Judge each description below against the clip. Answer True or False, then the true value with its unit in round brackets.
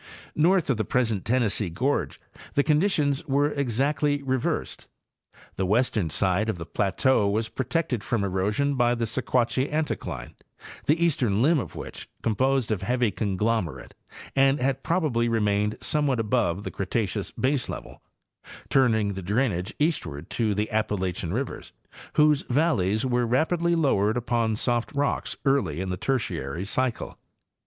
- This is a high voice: False (120 Hz)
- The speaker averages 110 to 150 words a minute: True (140 wpm)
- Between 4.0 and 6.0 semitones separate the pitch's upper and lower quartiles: True (5.1 semitones)